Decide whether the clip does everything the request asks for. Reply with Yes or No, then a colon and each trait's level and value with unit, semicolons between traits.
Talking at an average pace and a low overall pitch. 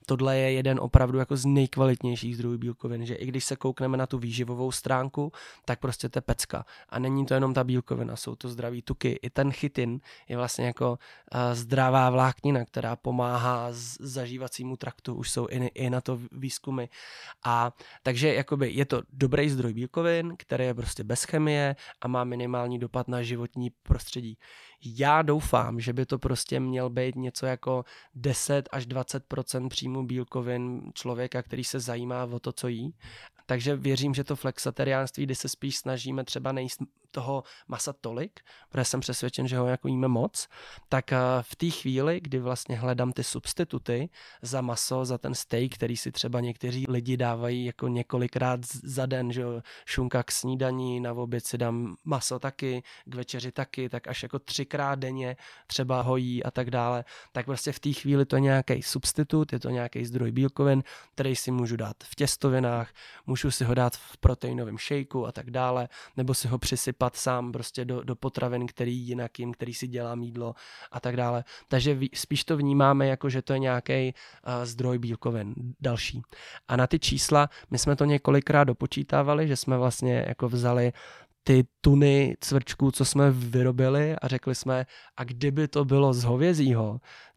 No: fast, 175 wpm; low, 130 Hz